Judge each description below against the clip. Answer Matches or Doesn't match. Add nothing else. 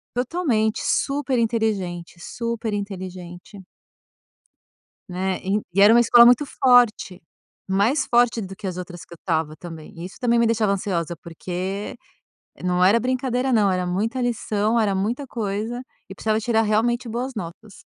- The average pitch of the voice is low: Doesn't match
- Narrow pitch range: Doesn't match